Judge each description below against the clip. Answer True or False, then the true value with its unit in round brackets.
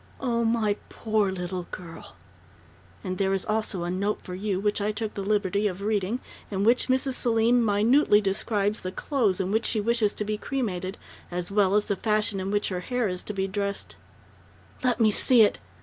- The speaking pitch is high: True (205 Hz)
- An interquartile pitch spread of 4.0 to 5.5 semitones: False (2.6 semitones)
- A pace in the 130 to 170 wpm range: False (205 wpm)